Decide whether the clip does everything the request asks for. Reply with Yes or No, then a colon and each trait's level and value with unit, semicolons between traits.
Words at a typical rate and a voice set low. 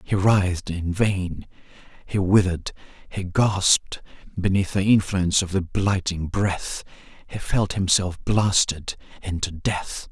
No: slow, 105 wpm; very low, 95 Hz